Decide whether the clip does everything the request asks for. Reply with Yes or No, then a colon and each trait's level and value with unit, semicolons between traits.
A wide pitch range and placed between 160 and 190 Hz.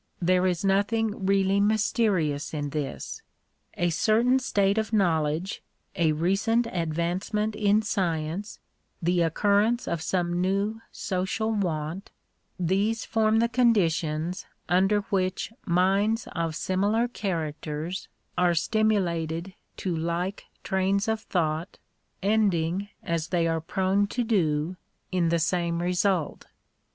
No: average, 3.8 semitones; medium, 185 Hz